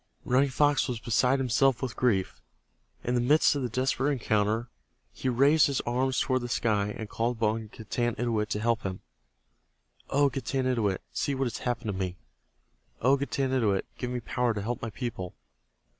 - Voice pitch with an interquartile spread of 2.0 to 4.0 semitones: Yes, average, 3.1 semitones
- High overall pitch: No, low, 120 Hz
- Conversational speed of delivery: Yes, average, 170 wpm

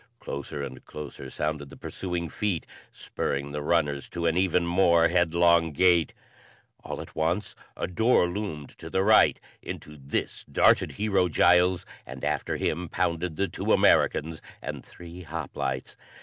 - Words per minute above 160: No, average, 150 wpm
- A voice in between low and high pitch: No, very low, 85 Hz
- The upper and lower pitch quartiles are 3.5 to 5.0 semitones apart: No, average, 2.9 semitones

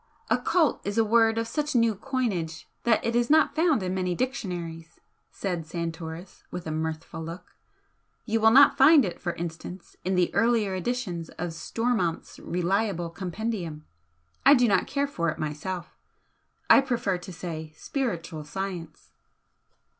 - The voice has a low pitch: No, medium, 185 Hz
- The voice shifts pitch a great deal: Yes, wide, 5.7 semitones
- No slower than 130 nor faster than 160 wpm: Yes, average, 150 wpm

